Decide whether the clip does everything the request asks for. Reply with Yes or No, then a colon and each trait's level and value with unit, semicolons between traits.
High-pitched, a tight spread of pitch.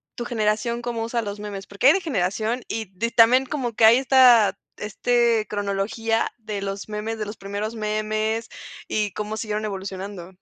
Yes: high, 215 Hz; narrow, 2.3 semitones